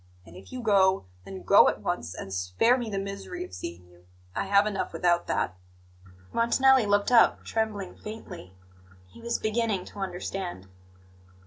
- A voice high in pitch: Yes, high, 200 Hz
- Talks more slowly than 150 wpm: No, average, 160 wpm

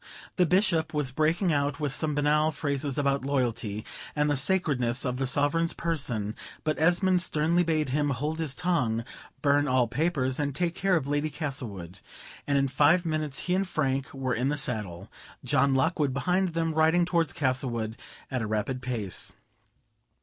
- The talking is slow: No, average, 170 wpm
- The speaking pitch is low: No, medium, 145 Hz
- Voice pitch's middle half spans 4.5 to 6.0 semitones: No, average, 4.0 semitones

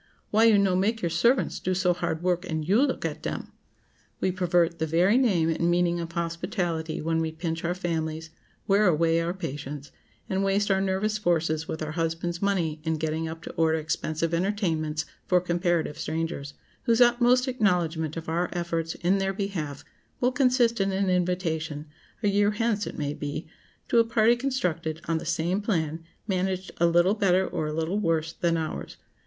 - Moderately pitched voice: Yes, medium, 175 Hz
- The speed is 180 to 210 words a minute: Yes, average, 185 wpm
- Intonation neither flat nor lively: Yes, average, 3.4 semitones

